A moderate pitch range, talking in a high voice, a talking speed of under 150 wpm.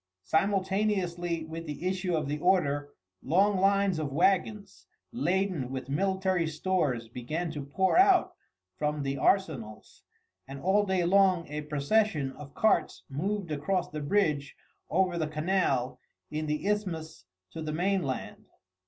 No: average, 4.5 semitones; medium, 170 Hz; slow, 135 wpm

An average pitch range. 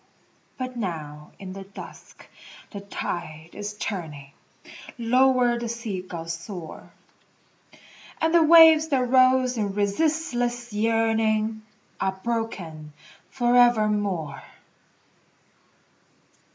Yes: average, 4.8 semitones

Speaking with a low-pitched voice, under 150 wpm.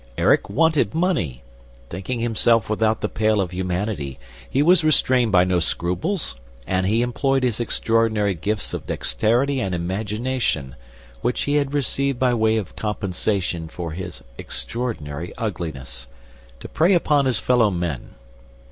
Yes: low, 110 Hz; average, 140 wpm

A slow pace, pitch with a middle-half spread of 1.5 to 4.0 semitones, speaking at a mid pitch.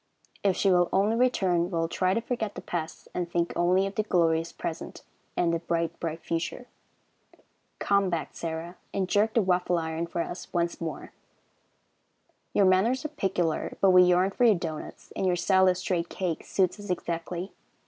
No: average, 185 wpm; narrow, 2.4 semitones; medium, 180 Hz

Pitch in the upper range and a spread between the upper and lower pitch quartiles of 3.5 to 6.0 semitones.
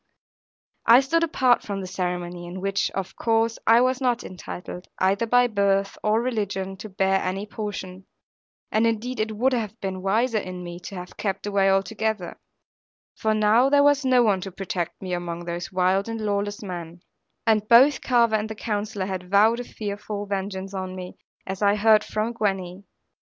No: high, 205 Hz; average, 3.1 semitones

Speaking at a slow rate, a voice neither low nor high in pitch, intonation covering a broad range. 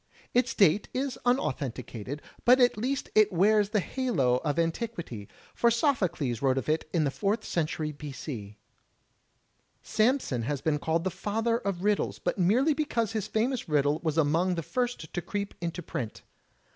No: average, 165 wpm; medium, 180 Hz; wide, 7.6 semitones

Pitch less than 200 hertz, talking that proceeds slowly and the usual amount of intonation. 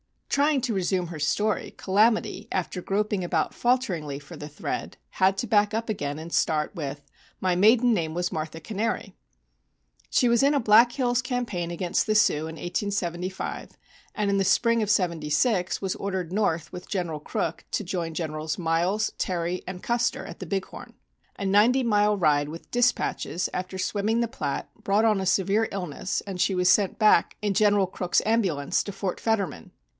No: high, 190 Hz; average, 180 wpm; average, 4.1 semitones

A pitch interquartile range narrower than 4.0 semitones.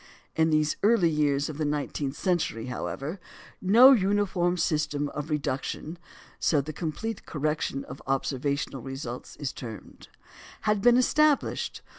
No: average, 5.0 semitones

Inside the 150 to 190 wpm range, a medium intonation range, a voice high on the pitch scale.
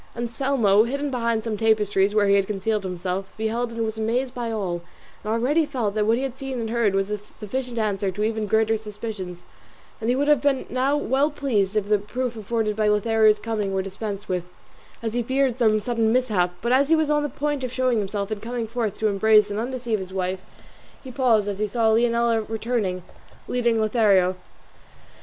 No: fast, 205 wpm; average, 3.0 semitones; high, 220 Hz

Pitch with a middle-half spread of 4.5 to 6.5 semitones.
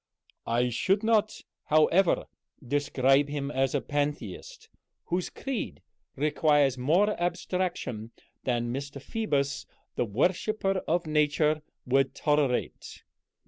Yes: average, 4.8 semitones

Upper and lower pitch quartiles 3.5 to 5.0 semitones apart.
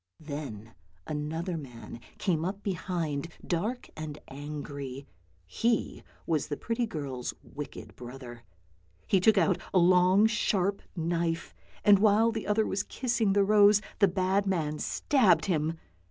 No: wide, 5.4 semitones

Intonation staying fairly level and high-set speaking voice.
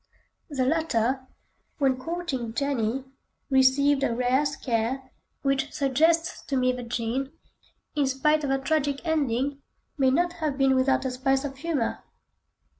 Yes: narrow, 2.0 semitones; very high, 270 Hz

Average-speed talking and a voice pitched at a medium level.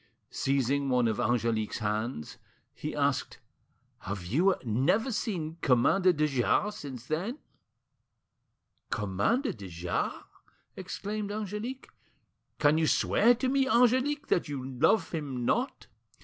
No: slow, 120 wpm; medium, 155 Hz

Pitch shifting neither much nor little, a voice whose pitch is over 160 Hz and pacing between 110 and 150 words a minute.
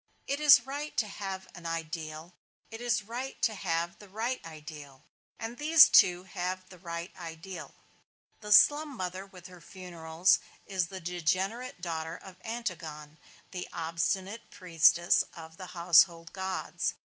Yes: average, 4.2 semitones; medium, 185 Hz; average, 145 wpm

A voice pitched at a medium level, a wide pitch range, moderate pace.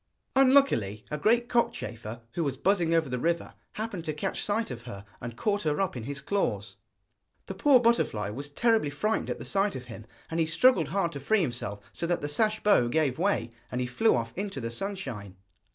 No: medium, 160 Hz; wide, 8.8 semitones; fast, 210 wpm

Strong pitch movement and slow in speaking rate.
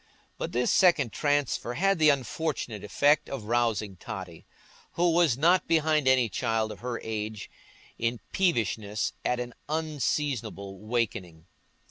Yes: wide, 5.9 semitones; slow, 130 wpm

